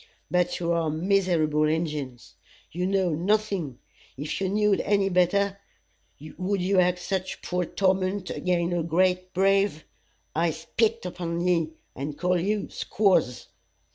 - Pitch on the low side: No, medium, 180 Hz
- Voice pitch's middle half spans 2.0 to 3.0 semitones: Yes, average, 2.7 semitones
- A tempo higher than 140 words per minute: No, slow, 135 wpm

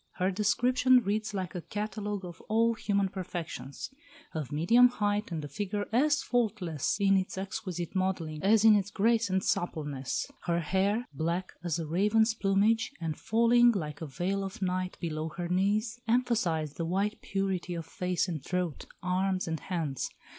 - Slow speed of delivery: No, average, 165 wpm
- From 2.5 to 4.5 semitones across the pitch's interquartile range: Yes, average, 3.9 semitones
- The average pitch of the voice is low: No, high, 190 Hz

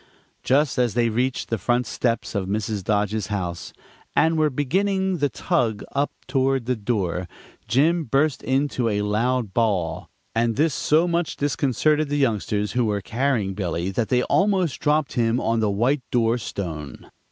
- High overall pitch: No, low, 120 Hz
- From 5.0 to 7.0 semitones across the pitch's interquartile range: Yes, wide, 5.4 semitones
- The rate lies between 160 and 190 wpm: Yes, average, 165 wpm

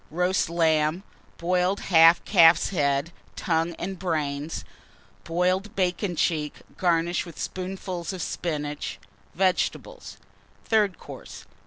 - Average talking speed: No, slow, 105 wpm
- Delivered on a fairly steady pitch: Yes, narrow, 2.2 semitones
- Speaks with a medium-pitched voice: Yes, medium, 175 Hz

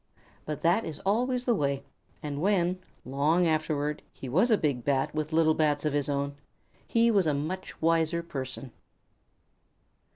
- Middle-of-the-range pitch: Yes, medium, 155 Hz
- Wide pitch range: No, average, 4.1 semitones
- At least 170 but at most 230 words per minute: No, average, 160 wpm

